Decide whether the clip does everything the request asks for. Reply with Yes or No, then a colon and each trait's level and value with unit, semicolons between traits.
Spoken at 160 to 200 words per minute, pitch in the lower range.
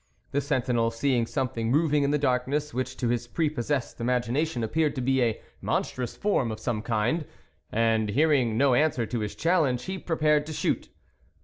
Yes: average, 175 wpm; low, 130 Hz